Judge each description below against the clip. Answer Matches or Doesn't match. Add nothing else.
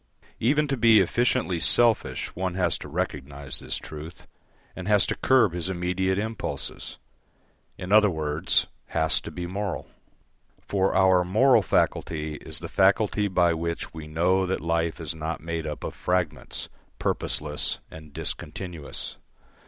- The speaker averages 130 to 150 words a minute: Matches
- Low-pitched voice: Matches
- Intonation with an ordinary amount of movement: Matches